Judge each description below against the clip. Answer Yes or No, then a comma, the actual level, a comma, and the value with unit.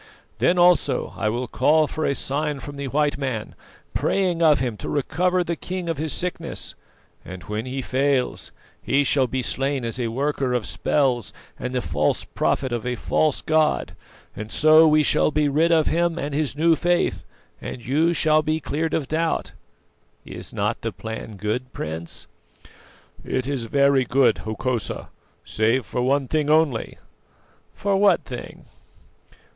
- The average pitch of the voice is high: No, medium, 140 Hz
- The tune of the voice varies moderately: Yes, average, 4.1 semitones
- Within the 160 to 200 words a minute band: Yes, average, 165 wpm